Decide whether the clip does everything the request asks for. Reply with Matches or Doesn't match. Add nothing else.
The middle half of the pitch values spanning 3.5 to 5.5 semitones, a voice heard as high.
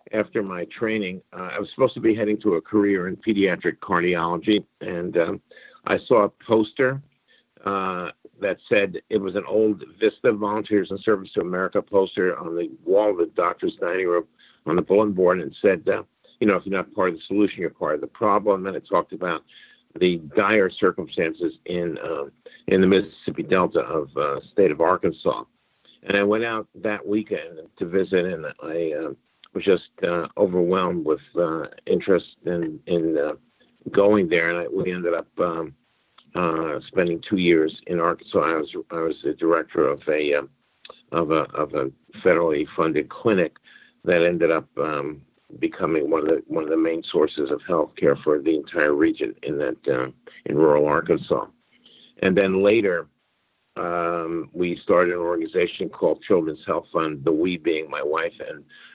Doesn't match